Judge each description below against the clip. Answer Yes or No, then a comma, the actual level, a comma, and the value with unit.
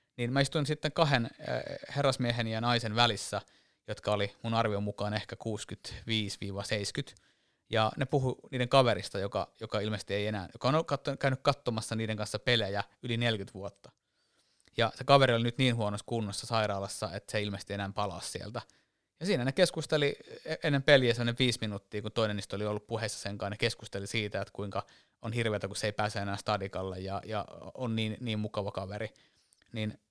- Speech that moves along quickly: Yes, fast, 175 wpm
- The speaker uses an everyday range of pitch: Yes, average, 3.0 semitones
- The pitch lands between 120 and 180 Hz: No, low, 110 Hz